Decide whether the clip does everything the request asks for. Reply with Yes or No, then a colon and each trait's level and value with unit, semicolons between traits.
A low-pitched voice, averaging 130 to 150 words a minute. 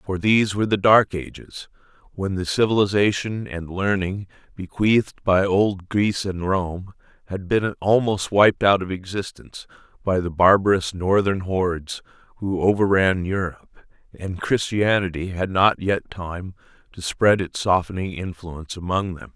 Yes: very low, 95 Hz; average, 140 wpm